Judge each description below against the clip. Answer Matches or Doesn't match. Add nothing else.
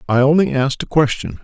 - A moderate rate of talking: Doesn't match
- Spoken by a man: Matches